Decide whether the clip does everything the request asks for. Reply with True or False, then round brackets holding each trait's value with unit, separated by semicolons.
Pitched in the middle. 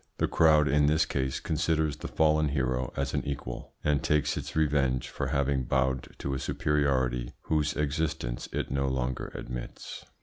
False (70 Hz)